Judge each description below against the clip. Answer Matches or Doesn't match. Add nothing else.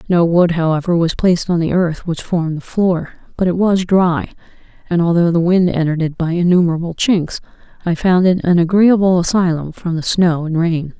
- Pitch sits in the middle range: Matches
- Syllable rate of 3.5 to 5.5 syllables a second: Matches